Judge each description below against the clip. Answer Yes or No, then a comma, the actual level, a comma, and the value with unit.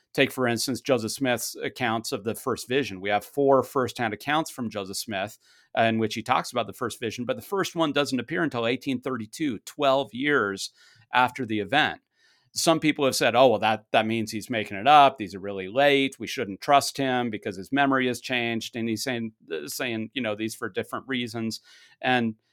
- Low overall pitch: Yes, low, 125 Hz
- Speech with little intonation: No, average, 3.3 semitones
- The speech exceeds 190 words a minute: Yes, average, 200 wpm